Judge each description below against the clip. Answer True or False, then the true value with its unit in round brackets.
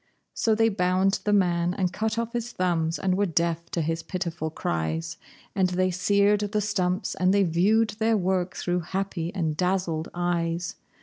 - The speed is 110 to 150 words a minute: False (175 wpm)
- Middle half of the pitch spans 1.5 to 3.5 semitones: True (3.0 semitones)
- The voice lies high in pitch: False (180 Hz)